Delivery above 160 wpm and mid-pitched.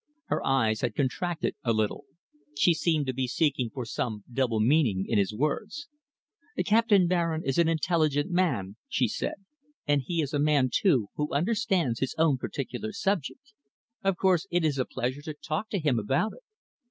Yes: average, 175 wpm; medium, 150 Hz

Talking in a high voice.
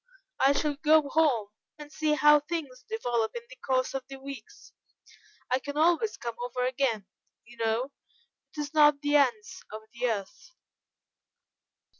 Yes: very high, 280 Hz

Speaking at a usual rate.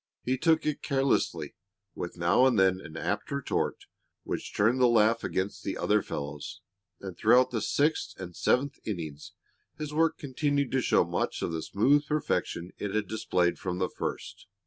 Yes: average, 170 wpm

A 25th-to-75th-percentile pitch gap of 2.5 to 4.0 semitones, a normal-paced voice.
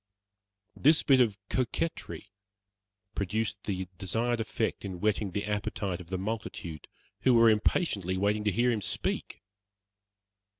No: average, 3.2 semitones; slow, 130 wpm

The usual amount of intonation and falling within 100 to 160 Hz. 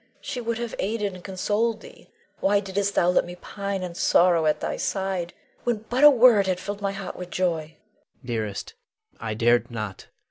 No: average, 3.6 semitones; high, 190 Hz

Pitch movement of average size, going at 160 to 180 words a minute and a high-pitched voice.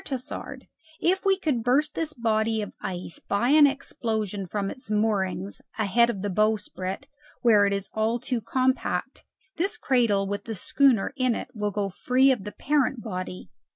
Yes: average, 4.3 semitones; average, 170 wpm; high, 220 Hz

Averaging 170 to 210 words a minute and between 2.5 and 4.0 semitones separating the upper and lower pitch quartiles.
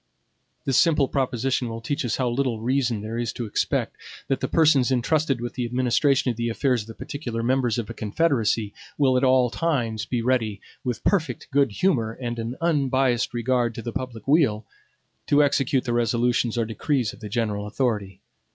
Yes: average, 190 wpm; average, 2.9 semitones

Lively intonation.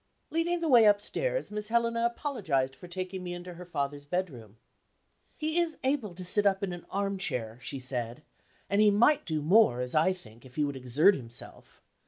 Yes: wide, 8.0 semitones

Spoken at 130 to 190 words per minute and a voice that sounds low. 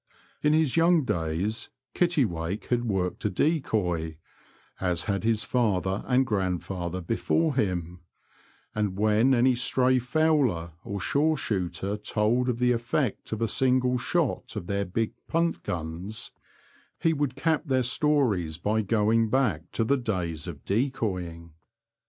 Yes: average, 140 wpm; low, 110 Hz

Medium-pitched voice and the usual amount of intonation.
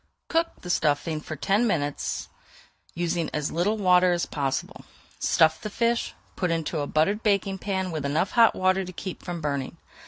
Yes: medium, 175 Hz; average, 4.0 semitones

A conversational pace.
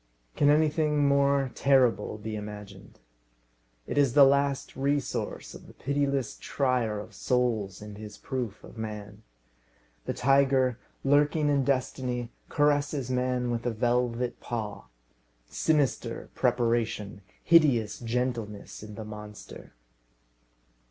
No: slow, 115 wpm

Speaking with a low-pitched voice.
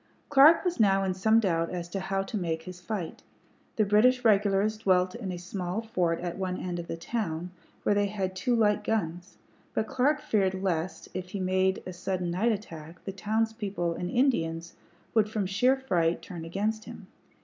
No: high, 195 Hz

